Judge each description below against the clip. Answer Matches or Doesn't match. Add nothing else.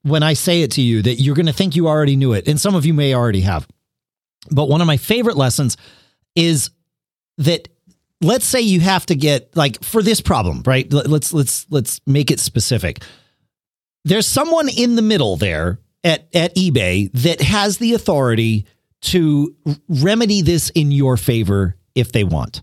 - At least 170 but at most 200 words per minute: Matches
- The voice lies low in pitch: Doesn't match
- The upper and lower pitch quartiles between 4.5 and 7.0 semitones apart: Matches